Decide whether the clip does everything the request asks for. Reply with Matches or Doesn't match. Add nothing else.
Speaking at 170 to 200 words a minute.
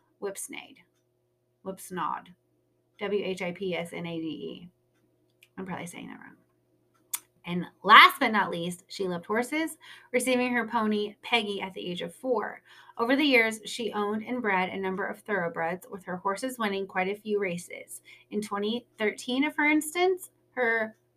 Doesn't match